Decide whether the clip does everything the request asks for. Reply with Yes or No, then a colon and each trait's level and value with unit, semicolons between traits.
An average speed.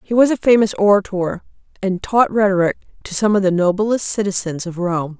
Yes: average, 185 wpm